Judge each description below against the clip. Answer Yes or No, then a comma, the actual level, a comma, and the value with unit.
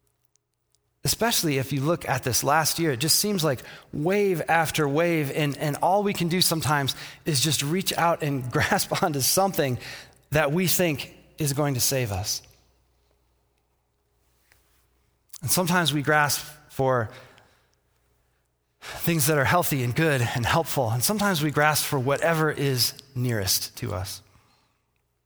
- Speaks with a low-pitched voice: No, medium, 145 Hz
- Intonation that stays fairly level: No, average, 5.3 semitones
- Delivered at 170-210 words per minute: No, average, 145 wpm